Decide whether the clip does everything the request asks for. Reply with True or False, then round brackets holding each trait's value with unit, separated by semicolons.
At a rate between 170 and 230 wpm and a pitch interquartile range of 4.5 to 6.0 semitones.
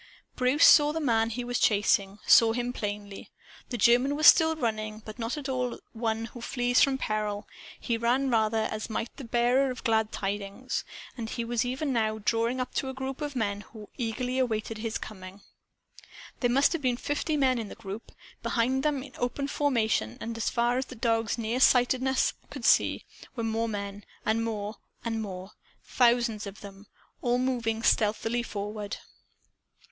False (185 wpm; 2.8 semitones)